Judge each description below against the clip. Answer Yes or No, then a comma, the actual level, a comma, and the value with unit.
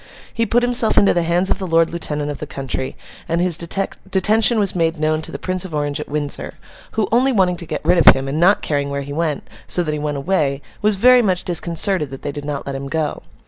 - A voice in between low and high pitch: Yes, medium, 165 Hz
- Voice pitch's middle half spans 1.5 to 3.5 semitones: No, average, 4.6 semitones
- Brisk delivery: Yes, fast, 245 wpm